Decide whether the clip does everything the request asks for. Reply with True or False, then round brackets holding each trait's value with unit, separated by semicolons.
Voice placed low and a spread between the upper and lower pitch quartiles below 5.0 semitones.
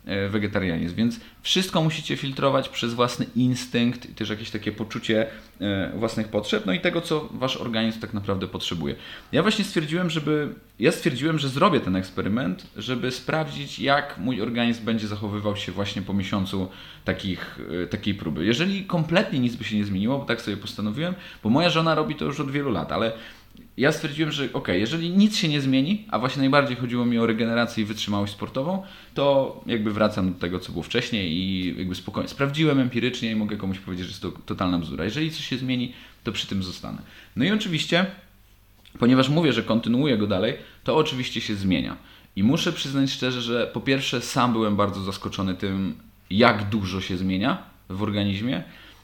False (115 Hz; 5.6 semitones)